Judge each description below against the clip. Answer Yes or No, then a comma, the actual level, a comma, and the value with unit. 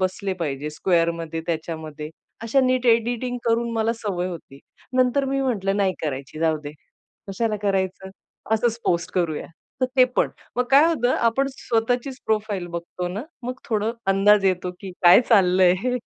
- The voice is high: Yes, high, 200 Hz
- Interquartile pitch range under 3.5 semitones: No, wide, 5.5 semitones